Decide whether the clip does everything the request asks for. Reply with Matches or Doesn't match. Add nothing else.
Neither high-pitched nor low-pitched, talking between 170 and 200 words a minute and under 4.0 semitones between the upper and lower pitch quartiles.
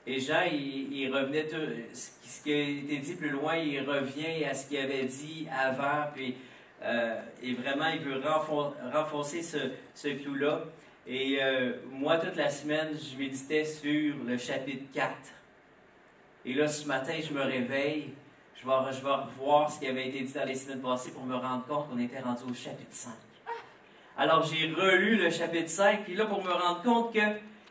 Matches